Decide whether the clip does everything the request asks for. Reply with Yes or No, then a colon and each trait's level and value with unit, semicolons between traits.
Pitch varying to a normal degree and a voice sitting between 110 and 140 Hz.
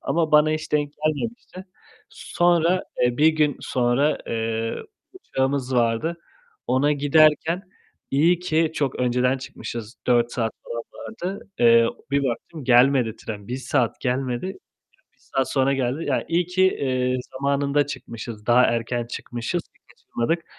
Yes: average, 4.4 semitones; low, 135 Hz